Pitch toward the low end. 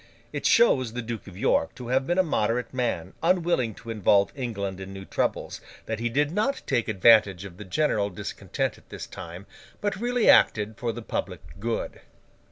Yes: low, 115 Hz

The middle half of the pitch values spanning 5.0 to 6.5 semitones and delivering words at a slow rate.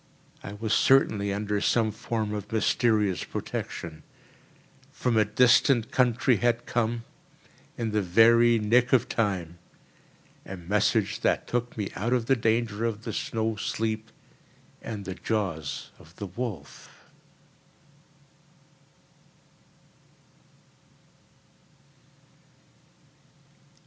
No: narrow, 2.5 semitones; slow, 100 wpm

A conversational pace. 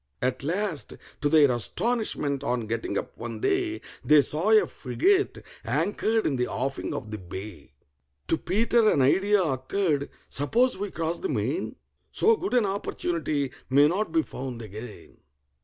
Yes: average, 155 wpm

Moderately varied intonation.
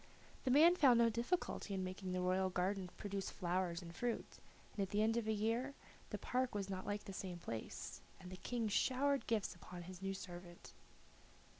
Yes: average, 4.2 semitones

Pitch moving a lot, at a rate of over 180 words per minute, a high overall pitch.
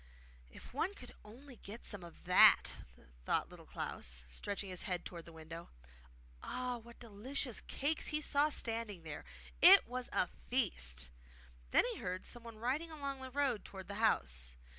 No: wide, 6.8 semitones; average, 160 wpm; high, 225 Hz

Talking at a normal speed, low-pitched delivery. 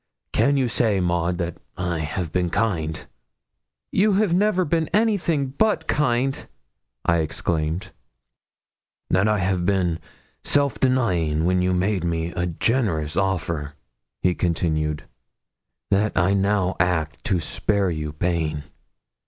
No: slow, 125 wpm; very low, 90 Hz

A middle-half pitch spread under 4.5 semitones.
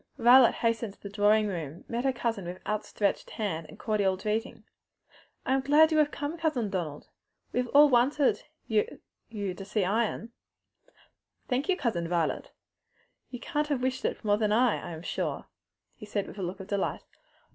No: average, 4.9 semitones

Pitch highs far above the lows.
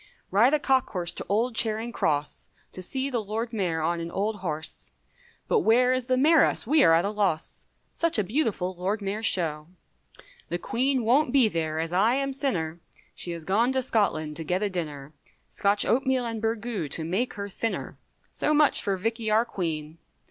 Yes: wide, 6.1 semitones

